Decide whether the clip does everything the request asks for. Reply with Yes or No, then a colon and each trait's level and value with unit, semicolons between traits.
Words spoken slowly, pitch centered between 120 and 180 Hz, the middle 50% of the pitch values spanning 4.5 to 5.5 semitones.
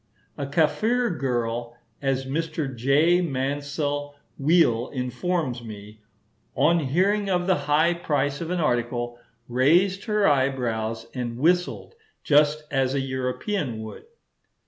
Yes: slow, 120 wpm; medium, 140 Hz; average, 5.2 semitones